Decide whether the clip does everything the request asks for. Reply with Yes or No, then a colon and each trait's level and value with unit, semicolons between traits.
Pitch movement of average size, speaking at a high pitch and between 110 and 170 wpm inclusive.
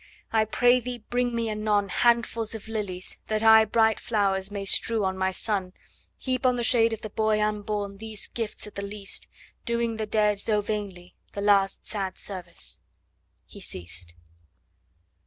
No: narrow, 2.1 semitones; high, 215 Hz; average, 165 wpm